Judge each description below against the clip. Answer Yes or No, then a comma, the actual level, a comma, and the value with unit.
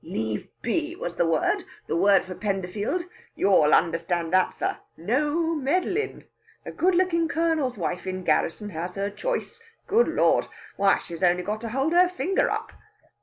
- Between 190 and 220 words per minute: No, average, 165 wpm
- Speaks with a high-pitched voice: Yes, high, 210 Hz